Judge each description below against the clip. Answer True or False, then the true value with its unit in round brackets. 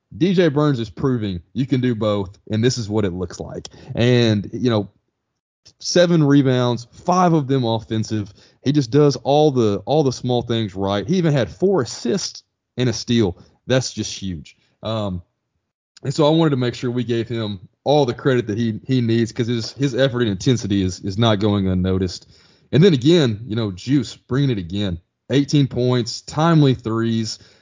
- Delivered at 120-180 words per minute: False (190 wpm)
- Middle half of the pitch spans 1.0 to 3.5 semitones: False (4.4 semitones)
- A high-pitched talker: False (120 Hz)